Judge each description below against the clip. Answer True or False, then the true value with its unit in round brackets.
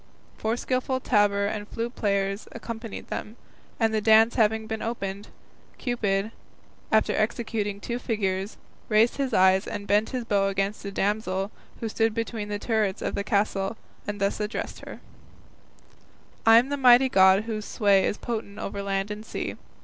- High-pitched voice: True (215 Hz)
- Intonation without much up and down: True (2.3 semitones)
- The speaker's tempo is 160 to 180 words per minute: True (165 wpm)